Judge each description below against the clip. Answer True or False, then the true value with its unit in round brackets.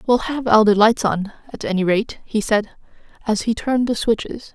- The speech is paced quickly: True (210 wpm)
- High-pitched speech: True (220 Hz)